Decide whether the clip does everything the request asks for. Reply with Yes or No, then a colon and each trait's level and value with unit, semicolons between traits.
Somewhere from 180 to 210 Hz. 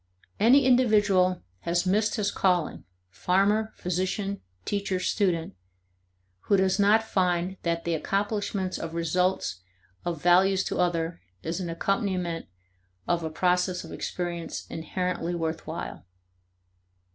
Yes: medium, 185 Hz